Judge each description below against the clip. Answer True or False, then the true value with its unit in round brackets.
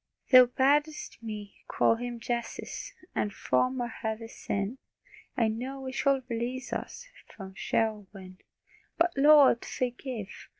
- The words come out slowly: True (130 wpm)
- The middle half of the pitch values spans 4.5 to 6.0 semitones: False (3.2 semitones)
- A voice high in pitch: True (240 Hz)